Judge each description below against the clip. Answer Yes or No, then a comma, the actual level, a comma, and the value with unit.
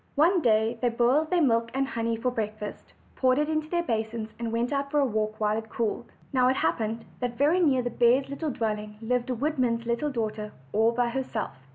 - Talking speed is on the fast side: Yes, fast, 215 wpm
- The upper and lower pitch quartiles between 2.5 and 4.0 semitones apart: Yes, average, 3.5 semitones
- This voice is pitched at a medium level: No, high, 235 Hz